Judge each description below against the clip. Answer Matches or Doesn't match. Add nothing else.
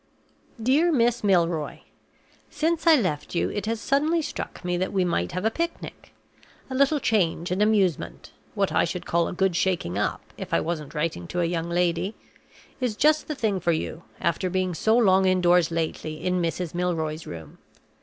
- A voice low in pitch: Doesn't match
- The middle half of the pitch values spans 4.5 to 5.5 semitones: Matches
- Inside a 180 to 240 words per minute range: Matches